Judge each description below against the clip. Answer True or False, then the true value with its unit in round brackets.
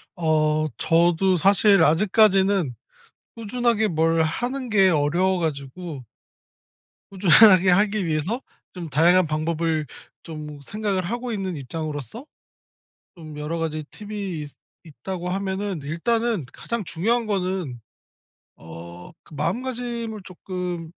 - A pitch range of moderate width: True (4.8 semitones)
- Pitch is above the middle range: False (180 Hz)